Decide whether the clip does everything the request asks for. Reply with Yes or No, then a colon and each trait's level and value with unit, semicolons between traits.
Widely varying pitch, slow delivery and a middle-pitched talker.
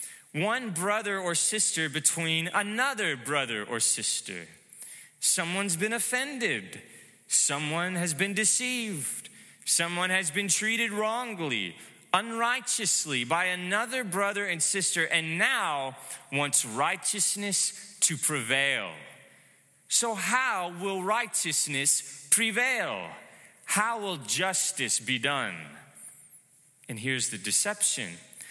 Yes: wide, 6.4 semitones; slow, 100 wpm; medium, 180 Hz